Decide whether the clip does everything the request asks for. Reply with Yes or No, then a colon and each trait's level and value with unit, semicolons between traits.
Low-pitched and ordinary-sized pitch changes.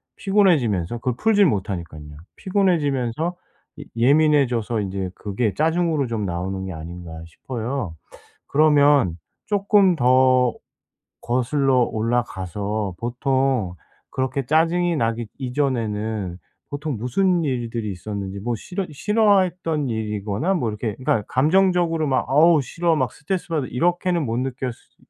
No: low, 130 Hz; wide, 6.8 semitones